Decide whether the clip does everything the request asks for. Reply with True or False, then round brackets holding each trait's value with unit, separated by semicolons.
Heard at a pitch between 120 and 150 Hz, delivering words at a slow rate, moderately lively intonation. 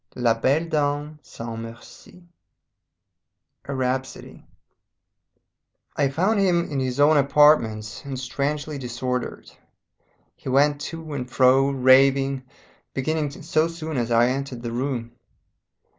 True (135 Hz; 115 wpm; 3.0 semitones)